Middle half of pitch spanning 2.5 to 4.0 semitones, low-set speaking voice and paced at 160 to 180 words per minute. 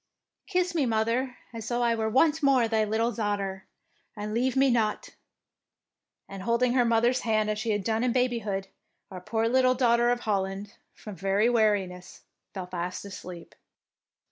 No: average, 3.2 semitones; high, 225 Hz; average, 170 wpm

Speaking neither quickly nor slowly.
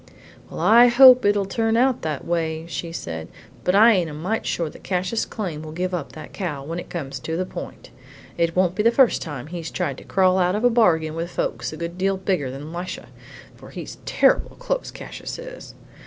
No: fast, 215 wpm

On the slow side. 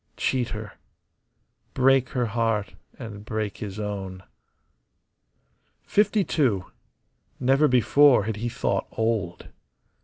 Yes: slow, 100 wpm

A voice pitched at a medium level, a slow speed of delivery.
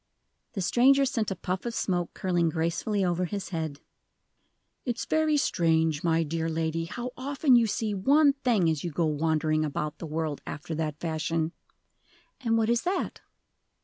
No: medium, 175 Hz; average, 165 wpm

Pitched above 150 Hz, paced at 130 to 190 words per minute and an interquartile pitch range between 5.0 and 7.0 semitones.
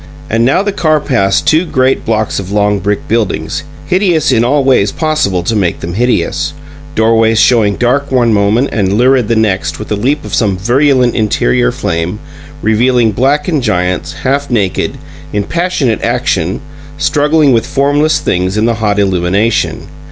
No: low, 115 Hz; average, 160 wpm; wide, 5.5 semitones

